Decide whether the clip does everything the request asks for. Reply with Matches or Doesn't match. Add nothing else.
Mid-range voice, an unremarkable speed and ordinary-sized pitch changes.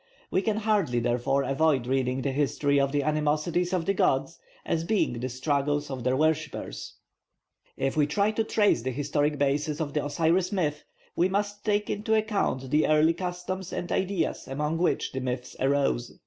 Matches